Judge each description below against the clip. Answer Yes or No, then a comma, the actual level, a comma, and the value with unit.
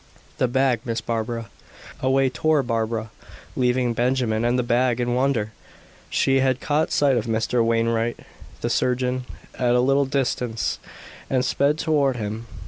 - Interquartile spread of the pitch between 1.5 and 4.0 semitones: Yes, narrow, 2.4 semitones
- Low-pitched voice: Yes, low, 125 Hz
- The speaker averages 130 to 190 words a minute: Yes, average, 145 wpm